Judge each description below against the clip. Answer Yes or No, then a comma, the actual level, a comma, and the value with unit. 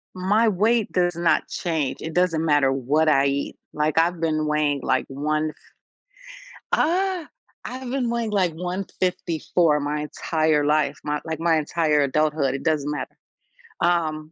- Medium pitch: Yes, medium, 160 Hz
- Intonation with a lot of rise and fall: No, average, 3.1 semitones